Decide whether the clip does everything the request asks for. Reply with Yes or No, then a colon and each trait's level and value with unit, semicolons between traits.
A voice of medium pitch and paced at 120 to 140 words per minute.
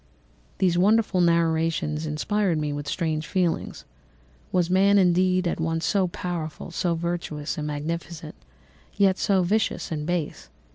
Yes: medium, 170 Hz; slow, 135 wpm